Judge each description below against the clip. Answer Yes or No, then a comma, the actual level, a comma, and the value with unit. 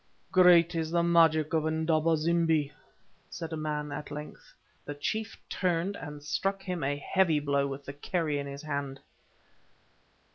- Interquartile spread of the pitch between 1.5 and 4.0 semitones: Yes, average, 2.7 semitones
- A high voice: No, medium, 155 Hz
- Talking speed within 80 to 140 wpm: No, average, 155 wpm